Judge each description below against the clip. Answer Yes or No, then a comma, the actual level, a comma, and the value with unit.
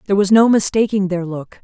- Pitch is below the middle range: No, high, 195 Hz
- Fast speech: Yes, fast, 220 wpm